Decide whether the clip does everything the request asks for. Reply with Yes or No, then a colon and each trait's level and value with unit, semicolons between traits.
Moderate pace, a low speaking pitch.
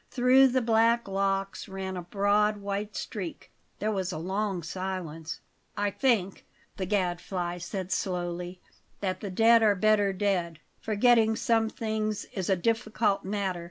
No: average, 145 wpm; high, 200 Hz